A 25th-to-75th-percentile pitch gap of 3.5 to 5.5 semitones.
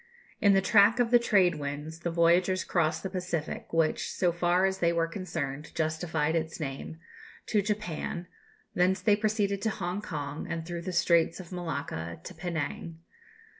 No: average, 3.0 semitones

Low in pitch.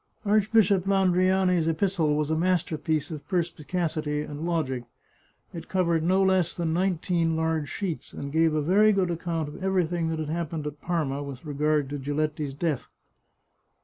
No: medium, 165 Hz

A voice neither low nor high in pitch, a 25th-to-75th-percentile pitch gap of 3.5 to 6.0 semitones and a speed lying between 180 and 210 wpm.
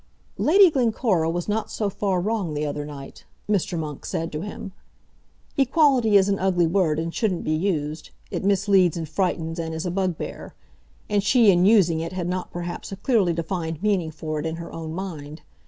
Yes: medium, 180 Hz; average, 3.9 semitones; average, 190 wpm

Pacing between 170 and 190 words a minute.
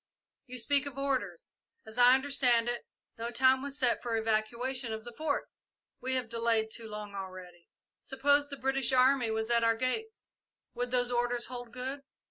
Yes: average, 180 wpm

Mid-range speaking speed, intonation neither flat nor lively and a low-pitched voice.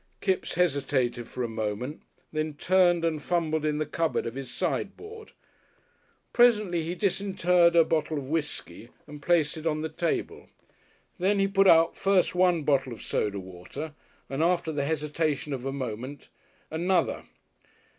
No: average, 155 wpm; average, 4.2 semitones; medium, 155 Hz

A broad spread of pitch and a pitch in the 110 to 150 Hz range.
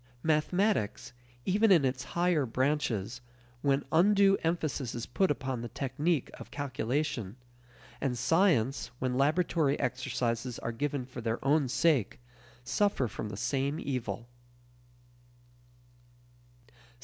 No: average, 4.7 semitones; low, 135 Hz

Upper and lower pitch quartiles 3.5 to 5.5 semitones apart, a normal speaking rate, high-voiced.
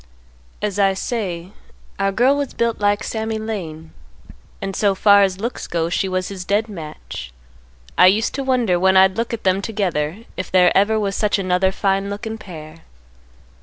No: average, 3.0 semitones; average, 175 wpm; high, 195 Hz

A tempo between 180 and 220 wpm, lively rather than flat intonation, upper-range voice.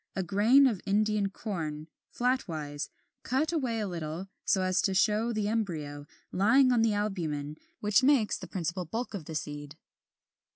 No: average, 160 wpm; wide, 5.9 semitones; high, 200 Hz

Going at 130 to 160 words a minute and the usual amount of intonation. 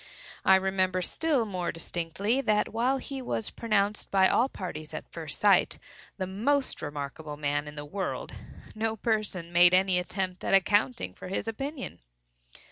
Yes: average, 155 wpm; average, 4.5 semitones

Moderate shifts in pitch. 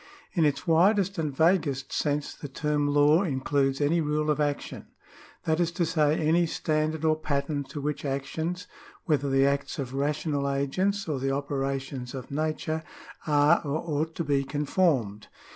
No: narrow, 2.3 semitones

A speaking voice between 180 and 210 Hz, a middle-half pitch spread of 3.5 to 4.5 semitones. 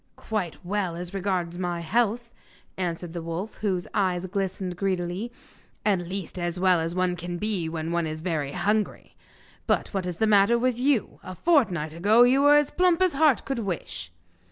Yes: medium, 185 Hz; average, 4.0 semitones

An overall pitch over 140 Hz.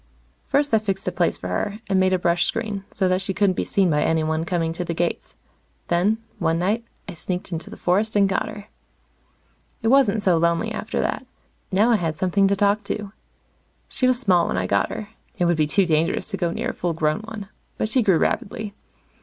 Yes: high, 190 Hz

